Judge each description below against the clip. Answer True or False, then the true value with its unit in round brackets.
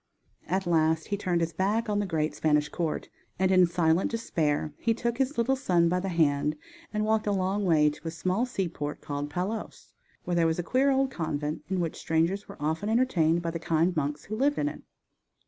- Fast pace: True (215 wpm)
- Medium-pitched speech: True (175 Hz)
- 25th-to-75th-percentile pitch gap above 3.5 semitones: True (4.7 semitones)